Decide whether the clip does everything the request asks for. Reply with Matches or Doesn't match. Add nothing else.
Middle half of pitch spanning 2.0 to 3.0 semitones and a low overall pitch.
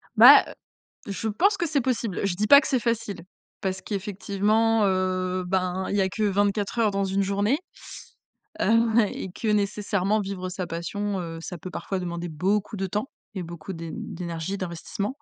Doesn't match